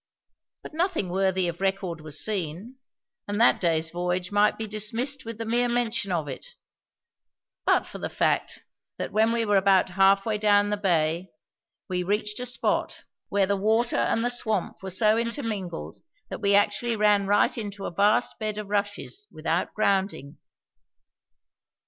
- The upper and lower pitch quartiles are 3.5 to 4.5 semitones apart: No, average, 3.0 semitones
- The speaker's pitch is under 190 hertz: No, high, 205 Hz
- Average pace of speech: Yes, average, 165 wpm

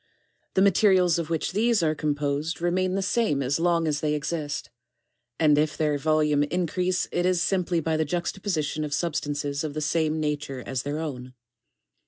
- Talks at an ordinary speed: Yes, average, 180 wpm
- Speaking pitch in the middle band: Yes, medium, 155 Hz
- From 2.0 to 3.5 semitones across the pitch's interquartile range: Yes, average, 3.1 semitones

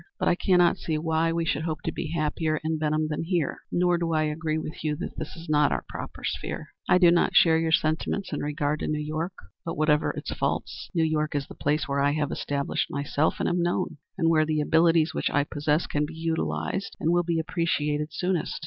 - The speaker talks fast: Yes, fast, 230 wpm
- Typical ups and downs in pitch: No, narrow, 1.8 semitones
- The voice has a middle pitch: Yes, medium, 155 Hz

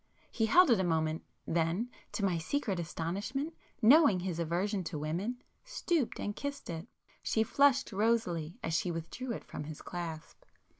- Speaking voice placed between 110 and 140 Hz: No, high, 190 Hz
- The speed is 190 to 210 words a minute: No, average, 155 wpm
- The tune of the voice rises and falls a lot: Yes, wide, 6.7 semitones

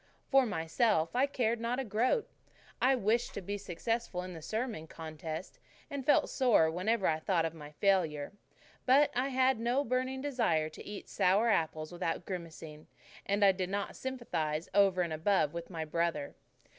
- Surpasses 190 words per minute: No, average, 175 wpm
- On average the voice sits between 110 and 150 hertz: No, high, 195 Hz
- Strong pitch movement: Yes, wide, 6.8 semitones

